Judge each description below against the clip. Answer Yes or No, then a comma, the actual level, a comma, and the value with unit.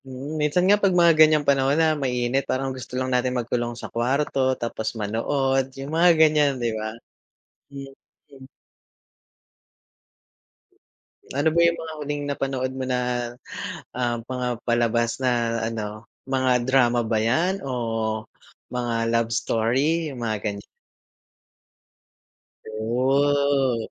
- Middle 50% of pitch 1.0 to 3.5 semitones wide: Yes, average, 3.2 semitones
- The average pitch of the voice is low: Yes, low, 130 Hz